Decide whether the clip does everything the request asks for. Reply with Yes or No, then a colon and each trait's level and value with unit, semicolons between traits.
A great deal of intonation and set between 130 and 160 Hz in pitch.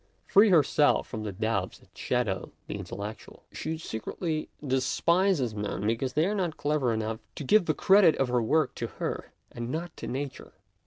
Yes: wide, 6.3 semitones; low, 135 Hz